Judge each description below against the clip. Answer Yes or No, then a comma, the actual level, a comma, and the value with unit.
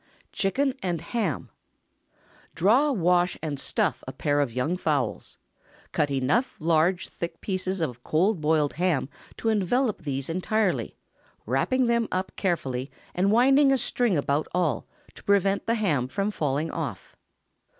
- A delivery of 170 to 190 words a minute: No, average, 145 wpm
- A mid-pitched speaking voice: Yes, medium, 180 Hz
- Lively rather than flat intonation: Yes, wide, 6.3 semitones